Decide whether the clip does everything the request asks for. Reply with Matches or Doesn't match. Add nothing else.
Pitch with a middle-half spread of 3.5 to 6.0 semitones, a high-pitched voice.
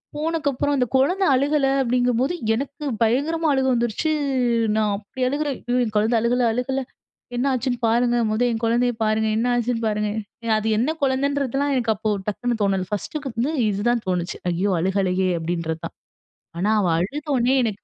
Matches